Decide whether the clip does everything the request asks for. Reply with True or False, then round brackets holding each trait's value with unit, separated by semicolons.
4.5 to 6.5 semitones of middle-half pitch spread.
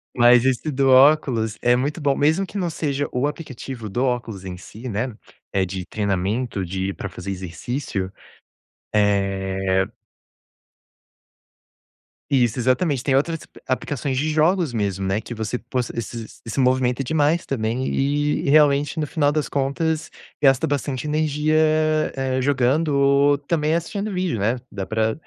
True (5.0 semitones)